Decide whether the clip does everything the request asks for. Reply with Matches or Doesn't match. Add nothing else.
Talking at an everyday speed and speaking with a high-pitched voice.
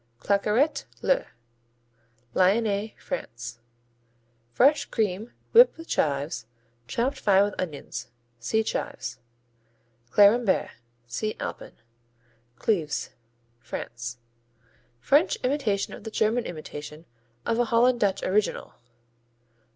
Doesn't match